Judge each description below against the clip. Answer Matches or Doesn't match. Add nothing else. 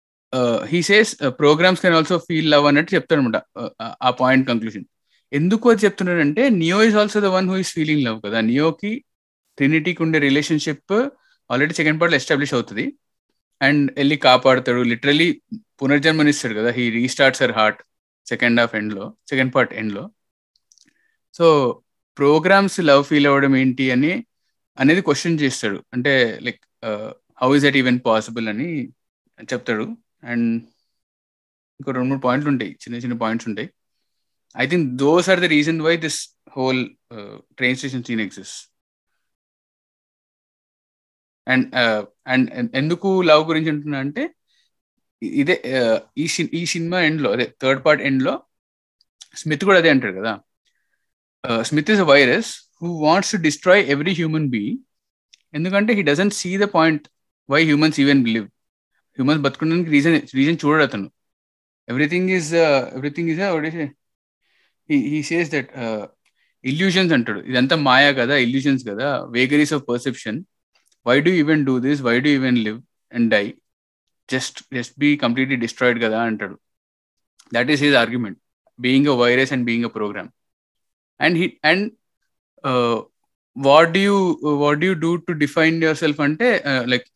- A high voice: Doesn't match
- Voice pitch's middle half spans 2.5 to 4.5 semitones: Doesn't match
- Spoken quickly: Matches